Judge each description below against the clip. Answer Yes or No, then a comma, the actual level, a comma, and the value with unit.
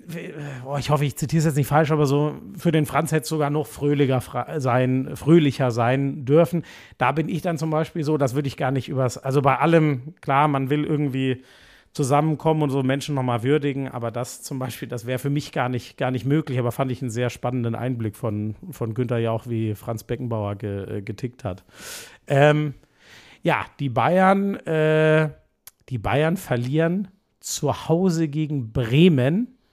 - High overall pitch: No, medium, 140 Hz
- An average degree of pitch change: Yes, average, 3.8 semitones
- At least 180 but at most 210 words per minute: Yes, average, 185 wpm